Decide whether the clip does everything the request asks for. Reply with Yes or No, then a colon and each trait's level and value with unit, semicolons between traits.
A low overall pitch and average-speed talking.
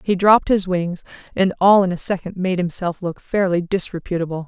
No: medium, 185 Hz; average, 190 wpm